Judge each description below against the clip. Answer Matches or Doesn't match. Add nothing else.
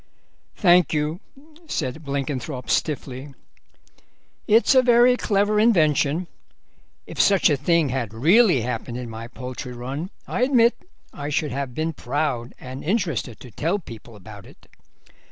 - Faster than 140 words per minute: Doesn't match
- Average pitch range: Doesn't match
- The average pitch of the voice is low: Doesn't match